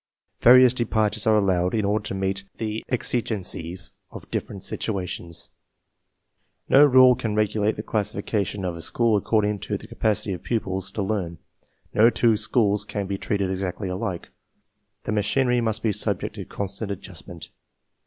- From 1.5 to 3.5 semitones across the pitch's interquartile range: Yes, narrow, 2.5 semitones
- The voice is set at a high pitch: No, low, 105 Hz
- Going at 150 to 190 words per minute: Yes, average, 160 wpm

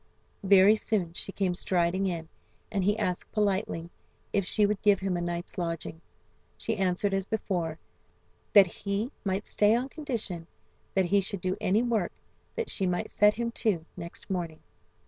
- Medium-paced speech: Yes, average, 165 wpm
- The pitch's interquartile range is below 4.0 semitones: Yes, average, 2.9 semitones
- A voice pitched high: Yes, high, 195 Hz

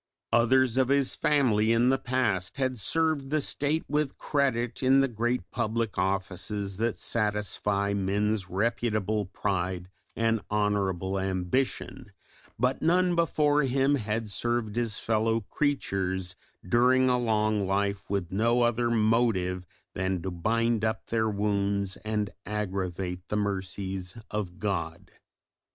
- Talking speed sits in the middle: No, slow, 130 wpm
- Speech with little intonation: No, average, 3.8 semitones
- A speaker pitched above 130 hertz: No, low, 110 Hz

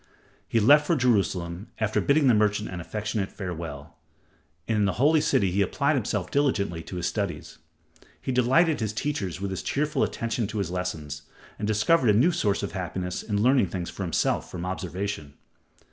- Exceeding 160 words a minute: Yes, average, 180 wpm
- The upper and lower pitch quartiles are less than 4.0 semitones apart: No, average, 5.1 semitones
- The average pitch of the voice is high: No, low, 100 Hz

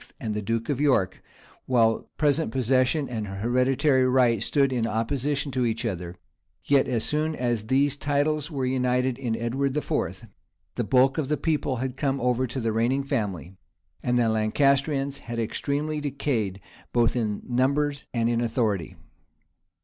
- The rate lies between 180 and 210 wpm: No, average, 155 wpm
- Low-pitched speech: Yes, low, 130 Hz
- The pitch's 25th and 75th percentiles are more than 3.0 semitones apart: Yes, average, 3.4 semitones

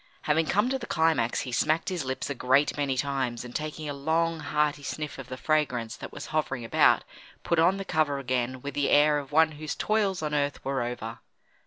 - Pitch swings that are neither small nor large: Yes, average, 3.3 semitones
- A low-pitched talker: No, medium, 145 Hz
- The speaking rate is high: Yes, fast, 215 wpm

